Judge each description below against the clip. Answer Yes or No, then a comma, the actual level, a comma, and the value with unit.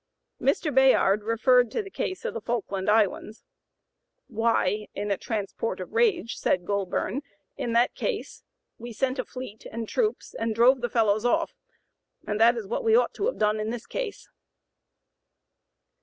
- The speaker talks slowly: No, average, 165 wpm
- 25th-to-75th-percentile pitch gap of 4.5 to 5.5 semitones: No, average, 4.0 semitones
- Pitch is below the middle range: No, high, 230 Hz